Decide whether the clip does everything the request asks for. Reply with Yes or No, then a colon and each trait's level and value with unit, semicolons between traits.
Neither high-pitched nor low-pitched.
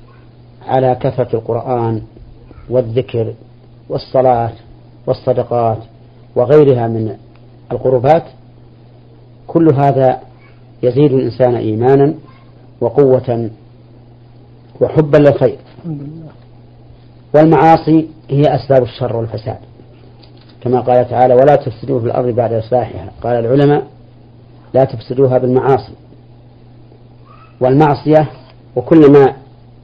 No: low, 125 Hz